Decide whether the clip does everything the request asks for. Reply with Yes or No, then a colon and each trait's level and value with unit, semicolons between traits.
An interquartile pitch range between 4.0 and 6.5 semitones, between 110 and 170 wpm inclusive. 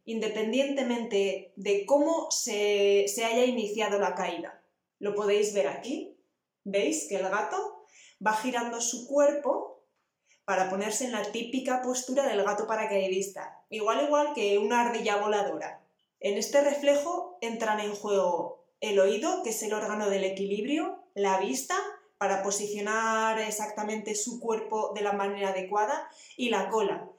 Yes: average, 4.3 semitones; average, 140 wpm